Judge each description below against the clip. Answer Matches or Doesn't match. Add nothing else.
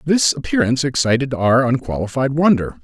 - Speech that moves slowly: Matches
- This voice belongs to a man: Matches